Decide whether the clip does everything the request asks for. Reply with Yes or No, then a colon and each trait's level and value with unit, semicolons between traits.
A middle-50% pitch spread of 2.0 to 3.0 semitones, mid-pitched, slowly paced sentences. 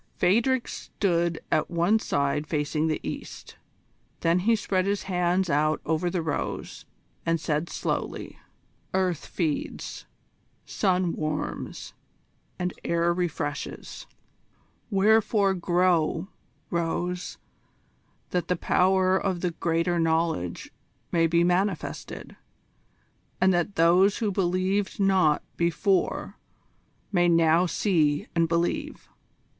Yes: narrow, 2.4 semitones; medium, 175 Hz; slow, 105 wpm